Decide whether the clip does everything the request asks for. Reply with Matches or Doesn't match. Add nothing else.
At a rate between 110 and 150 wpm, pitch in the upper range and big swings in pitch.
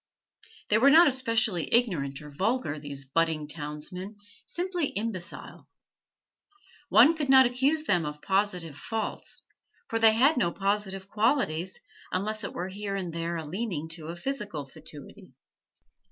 Matches